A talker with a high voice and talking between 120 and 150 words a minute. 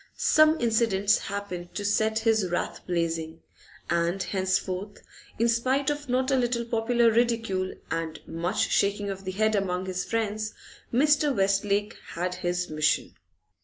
Yes: high, 205 Hz; average, 140 wpm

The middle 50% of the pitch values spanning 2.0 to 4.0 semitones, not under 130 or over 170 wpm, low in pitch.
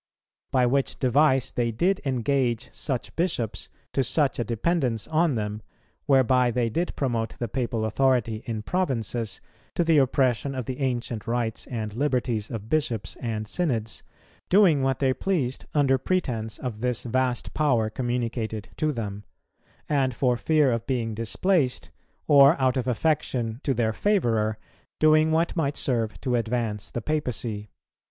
Yes: average, 3.7 semitones; average, 150 wpm; low, 125 Hz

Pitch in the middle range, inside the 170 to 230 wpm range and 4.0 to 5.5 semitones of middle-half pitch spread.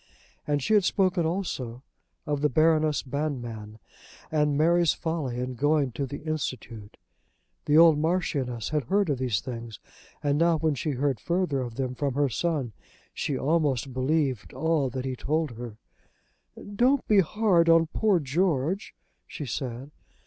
No: medium, 145 Hz; average, 155 wpm; average, 4.4 semitones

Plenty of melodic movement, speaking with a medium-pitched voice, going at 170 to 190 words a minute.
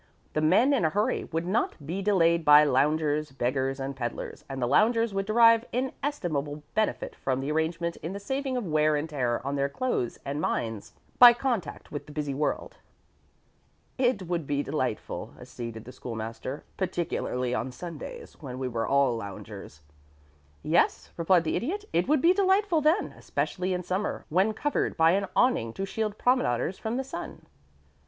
Yes: wide, 8.3 semitones; medium, 165 Hz; average, 175 wpm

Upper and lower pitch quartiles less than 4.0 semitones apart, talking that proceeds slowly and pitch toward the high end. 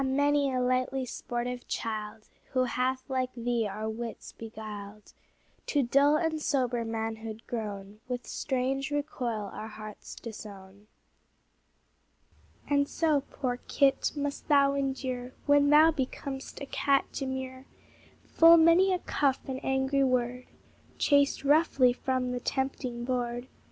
Yes: average, 3.0 semitones; slow, 125 wpm; very high, 255 Hz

